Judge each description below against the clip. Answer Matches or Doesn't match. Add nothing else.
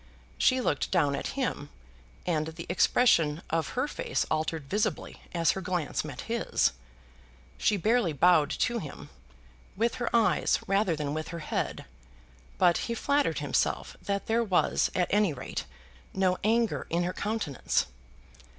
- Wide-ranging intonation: Matches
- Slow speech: Doesn't match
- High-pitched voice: Doesn't match